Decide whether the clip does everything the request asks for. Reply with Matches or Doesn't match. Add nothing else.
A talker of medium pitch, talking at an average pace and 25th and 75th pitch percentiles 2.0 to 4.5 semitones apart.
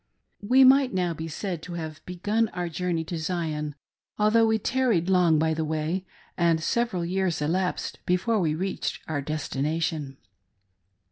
Matches